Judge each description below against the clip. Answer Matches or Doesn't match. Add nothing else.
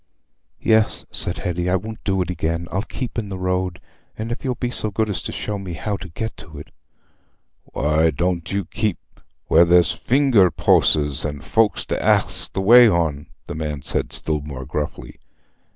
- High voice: Doesn't match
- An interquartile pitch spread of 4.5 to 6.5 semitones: Matches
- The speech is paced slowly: Doesn't match